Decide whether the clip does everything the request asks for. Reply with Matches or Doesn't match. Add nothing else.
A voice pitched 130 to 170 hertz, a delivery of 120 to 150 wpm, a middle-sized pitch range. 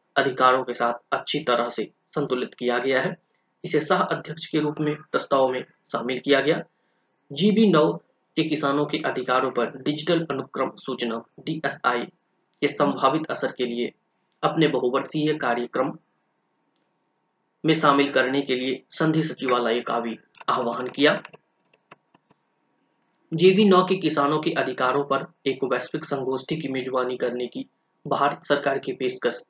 Matches